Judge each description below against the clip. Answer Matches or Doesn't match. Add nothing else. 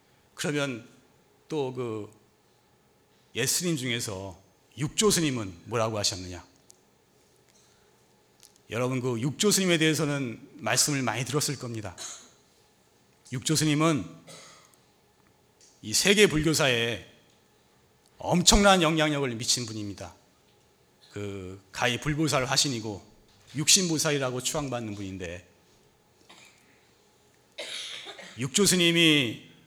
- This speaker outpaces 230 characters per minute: Doesn't match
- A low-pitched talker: Matches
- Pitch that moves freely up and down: Matches